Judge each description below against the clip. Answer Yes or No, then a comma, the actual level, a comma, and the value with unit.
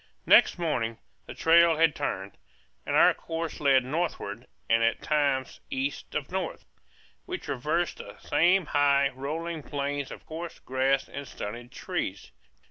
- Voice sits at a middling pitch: Yes, medium, 145 Hz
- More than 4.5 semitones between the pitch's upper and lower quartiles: No, average, 3.8 semitones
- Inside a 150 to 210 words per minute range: No, average, 140 wpm